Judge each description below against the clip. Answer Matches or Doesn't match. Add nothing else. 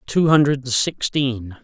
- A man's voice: Matches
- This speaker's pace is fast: Doesn't match